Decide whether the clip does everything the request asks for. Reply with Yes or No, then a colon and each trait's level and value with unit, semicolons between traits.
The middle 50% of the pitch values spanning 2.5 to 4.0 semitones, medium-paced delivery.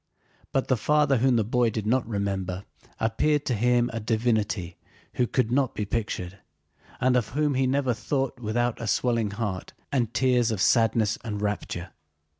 Yes: average, 3.2 semitones; average, 170 wpm